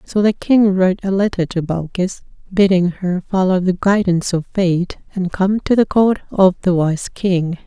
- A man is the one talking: No, female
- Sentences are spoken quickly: No, average, 190 wpm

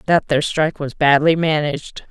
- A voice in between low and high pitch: Yes, medium, 150 Hz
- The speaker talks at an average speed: Yes, average, 170 wpm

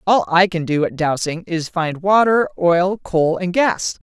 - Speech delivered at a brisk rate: No, average, 190 wpm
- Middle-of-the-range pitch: Yes, medium, 175 Hz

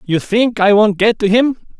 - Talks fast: Yes, fast, 235 wpm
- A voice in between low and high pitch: No, high, 215 Hz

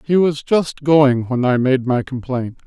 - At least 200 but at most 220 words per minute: Yes, fast, 205 wpm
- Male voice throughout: Yes, male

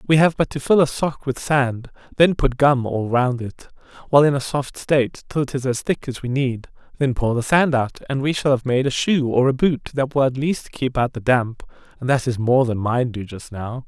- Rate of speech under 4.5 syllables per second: No, 5.1 syllables/s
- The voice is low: Yes, low, 130 Hz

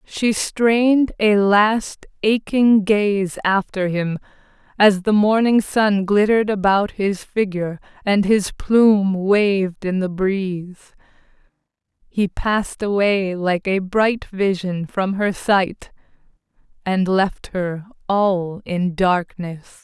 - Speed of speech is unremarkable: No, slow, 120 wpm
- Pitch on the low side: No, high, 200 Hz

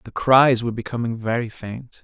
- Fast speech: No, average, 175 wpm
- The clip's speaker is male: Yes, male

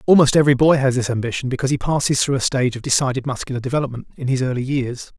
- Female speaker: No, male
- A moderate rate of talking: No, fast, 230 wpm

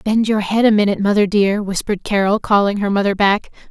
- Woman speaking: Yes, female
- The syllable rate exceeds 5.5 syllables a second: Yes, 6.1 syllables/s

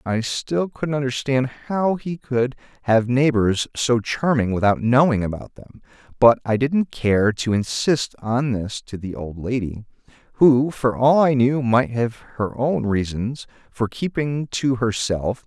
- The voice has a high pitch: No, low, 125 Hz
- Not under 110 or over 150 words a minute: No, average, 160 wpm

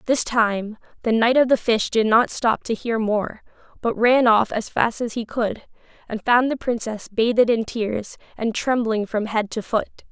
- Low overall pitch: No, high, 225 Hz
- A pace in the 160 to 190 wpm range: No, average, 200 wpm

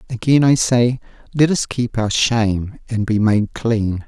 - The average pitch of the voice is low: Yes, low, 115 Hz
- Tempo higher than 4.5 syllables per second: No, 4.1 syllables/s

